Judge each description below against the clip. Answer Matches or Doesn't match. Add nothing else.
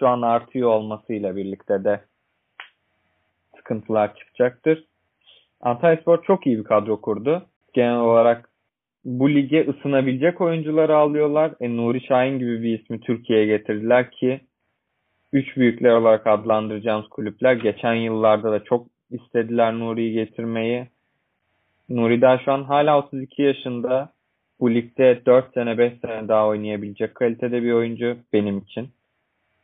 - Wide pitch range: Doesn't match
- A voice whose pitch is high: Doesn't match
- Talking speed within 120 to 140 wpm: Matches